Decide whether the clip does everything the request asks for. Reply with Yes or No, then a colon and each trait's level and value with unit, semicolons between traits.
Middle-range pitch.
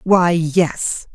Yes: medium, 170 Hz